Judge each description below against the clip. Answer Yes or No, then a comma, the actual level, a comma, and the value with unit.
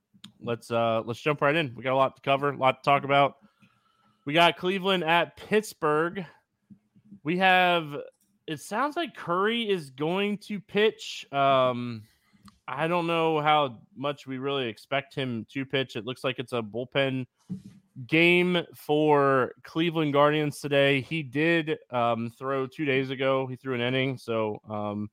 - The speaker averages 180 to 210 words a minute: No, average, 160 wpm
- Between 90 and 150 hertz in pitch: Yes, medium, 140 Hz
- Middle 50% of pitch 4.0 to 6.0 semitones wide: Yes, average, 4.5 semitones